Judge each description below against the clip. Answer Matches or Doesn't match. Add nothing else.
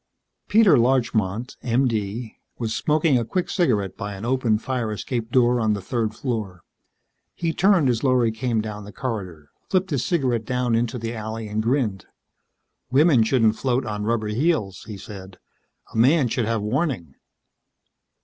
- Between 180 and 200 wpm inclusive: Doesn't match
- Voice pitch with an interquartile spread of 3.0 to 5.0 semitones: Matches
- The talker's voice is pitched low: Matches